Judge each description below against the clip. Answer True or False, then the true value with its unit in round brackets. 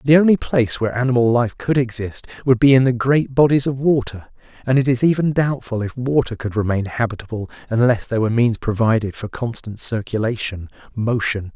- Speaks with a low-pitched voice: True (120 Hz)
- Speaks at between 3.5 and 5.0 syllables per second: False (5.8 syllables/s)